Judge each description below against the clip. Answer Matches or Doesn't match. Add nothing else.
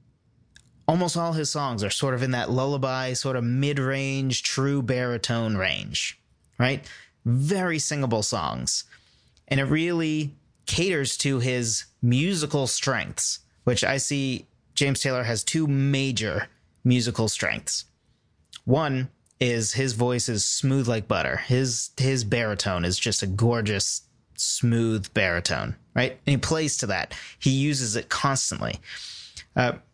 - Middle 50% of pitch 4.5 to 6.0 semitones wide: Doesn't match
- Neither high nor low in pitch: Doesn't match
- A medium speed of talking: Doesn't match